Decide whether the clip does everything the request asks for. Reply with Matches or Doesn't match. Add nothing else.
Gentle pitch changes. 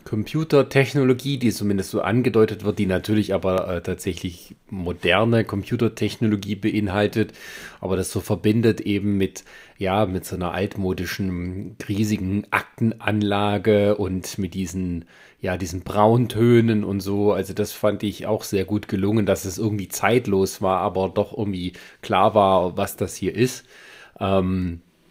Matches